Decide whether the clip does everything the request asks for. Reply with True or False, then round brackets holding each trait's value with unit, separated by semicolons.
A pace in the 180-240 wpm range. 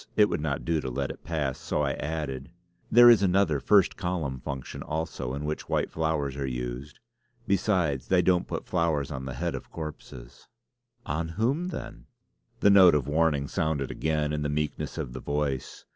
True (185 wpm)